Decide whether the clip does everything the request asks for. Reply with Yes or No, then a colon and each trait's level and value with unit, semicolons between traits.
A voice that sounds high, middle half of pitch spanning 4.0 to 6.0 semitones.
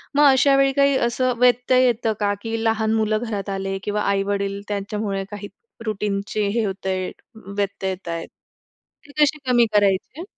No: high, 210 Hz; average, 3.3 semitones